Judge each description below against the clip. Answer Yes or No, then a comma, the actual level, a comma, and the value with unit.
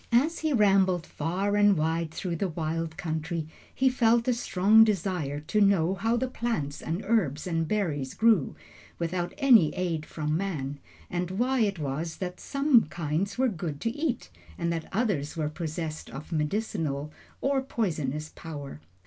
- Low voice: No, medium, 175 Hz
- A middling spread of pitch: No, wide, 5.9 semitones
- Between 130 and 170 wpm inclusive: Yes, average, 160 wpm